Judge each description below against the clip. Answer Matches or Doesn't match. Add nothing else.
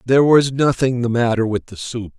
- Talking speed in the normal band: Doesn't match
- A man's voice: Matches